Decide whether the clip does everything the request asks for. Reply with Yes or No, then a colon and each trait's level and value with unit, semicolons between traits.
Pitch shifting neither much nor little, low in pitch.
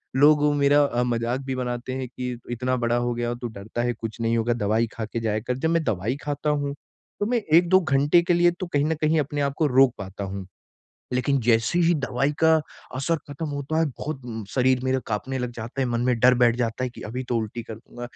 Yes: average, 3.5 semitones; low, 125 Hz